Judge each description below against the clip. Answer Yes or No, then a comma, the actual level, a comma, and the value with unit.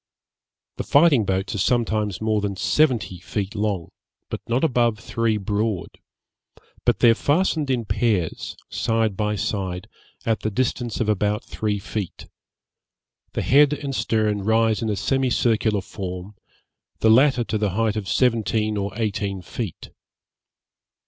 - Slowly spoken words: No, average, 145 wpm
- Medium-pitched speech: No, low, 110 Hz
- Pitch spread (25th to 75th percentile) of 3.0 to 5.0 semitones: No, narrow, 2.5 semitones